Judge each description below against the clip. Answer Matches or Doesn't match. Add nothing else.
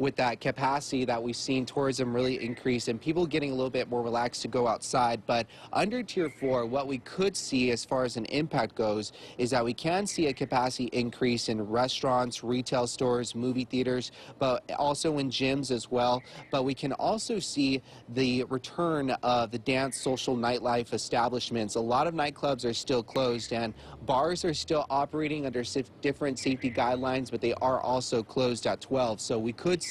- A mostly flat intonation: Matches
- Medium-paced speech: Matches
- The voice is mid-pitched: Doesn't match